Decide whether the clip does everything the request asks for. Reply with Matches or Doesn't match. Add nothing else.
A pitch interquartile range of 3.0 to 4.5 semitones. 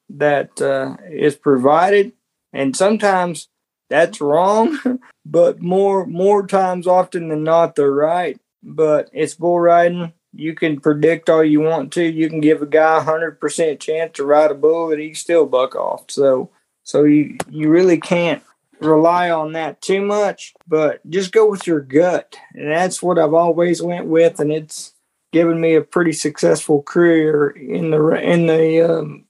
Doesn't match